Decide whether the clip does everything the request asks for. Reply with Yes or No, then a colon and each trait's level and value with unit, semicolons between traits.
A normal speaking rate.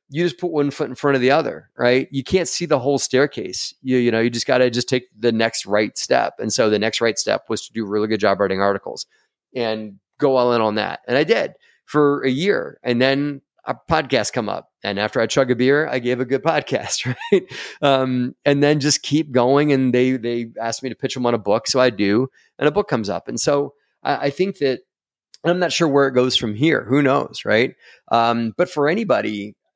No: fast, 245 wpm